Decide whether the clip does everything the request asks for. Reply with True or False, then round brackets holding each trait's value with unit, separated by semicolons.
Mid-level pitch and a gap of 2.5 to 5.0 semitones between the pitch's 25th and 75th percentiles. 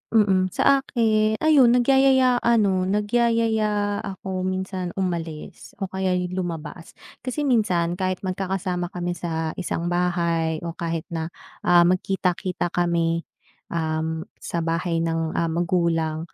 True (180 Hz; 3.6 semitones)